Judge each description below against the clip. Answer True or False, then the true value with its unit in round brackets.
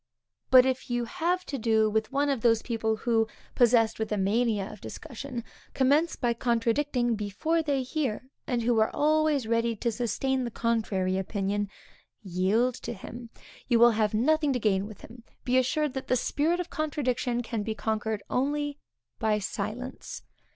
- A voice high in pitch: True (235 Hz)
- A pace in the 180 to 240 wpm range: False (170 wpm)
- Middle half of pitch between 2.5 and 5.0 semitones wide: True (3.5 semitones)